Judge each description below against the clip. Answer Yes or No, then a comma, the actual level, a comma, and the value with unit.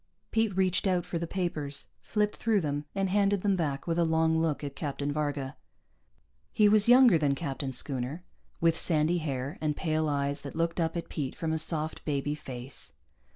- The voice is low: No, medium, 160 Hz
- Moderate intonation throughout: Yes, average, 3.8 semitones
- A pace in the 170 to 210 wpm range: Yes, average, 190 wpm